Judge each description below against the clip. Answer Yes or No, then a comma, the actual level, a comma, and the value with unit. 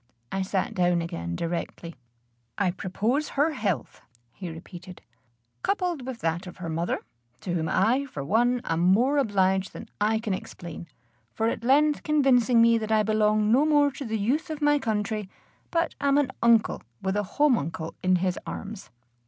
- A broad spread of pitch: Yes, wide, 6.2 semitones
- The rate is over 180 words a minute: No, average, 170 wpm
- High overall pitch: Yes, high, 215 Hz